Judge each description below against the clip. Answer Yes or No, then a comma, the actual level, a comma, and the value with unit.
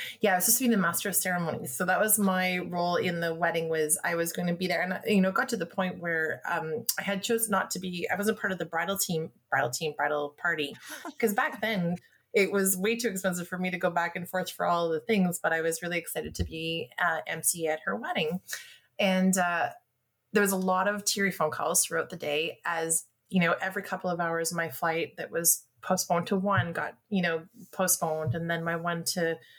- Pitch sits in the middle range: Yes, medium, 175 Hz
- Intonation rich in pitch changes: No, average, 2.9 semitones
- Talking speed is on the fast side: Yes, fast, 245 wpm